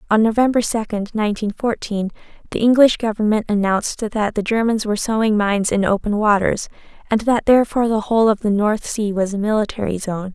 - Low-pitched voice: No, high, 215 Hz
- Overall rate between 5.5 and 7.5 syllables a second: Yes, 5.8 syllables/s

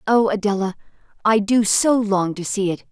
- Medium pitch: No, high, 205 Hz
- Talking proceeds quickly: No, average, 185 wpm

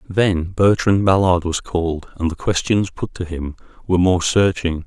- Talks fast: No, average, 175 wpm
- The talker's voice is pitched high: No, very low, 90 Hz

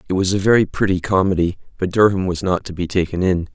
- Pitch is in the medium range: No, very low, 95 Hz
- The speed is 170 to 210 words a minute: No, fast, 235 wpm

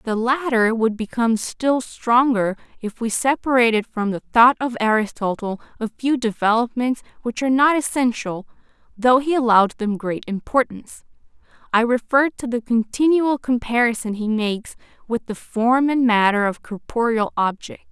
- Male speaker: No, female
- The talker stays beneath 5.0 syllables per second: Yes, 4.8 syllables/s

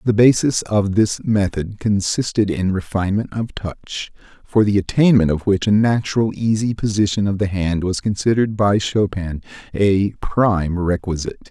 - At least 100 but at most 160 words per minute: Yes, average, 150 wpm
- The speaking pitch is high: No, low, 100 Hz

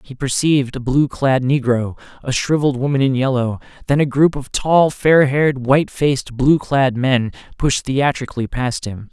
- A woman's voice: No, male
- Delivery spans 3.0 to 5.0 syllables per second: Yes, 4.9 syllables/s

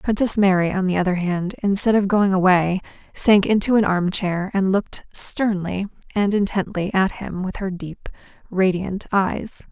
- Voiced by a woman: Yes, female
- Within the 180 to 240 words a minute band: No, average, 160 wpm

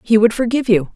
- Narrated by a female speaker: Yes, female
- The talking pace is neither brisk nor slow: No, fast, 250 wpm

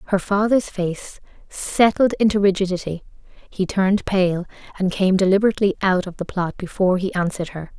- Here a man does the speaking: No, female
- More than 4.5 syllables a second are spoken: Yes, 5.6 syllables/s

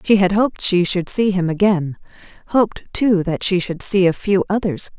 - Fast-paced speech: No, average, 190 wpm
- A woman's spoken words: Yes, female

